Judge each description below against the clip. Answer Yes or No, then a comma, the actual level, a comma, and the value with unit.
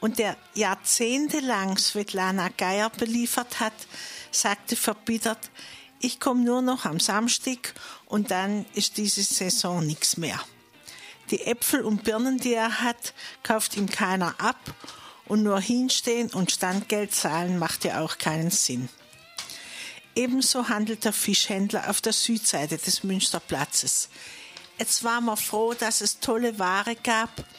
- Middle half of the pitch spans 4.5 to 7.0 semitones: No, average, 3.3 semitones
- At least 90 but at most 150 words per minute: Yes, average, 135 wpm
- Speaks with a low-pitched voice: No, high, 220 Hz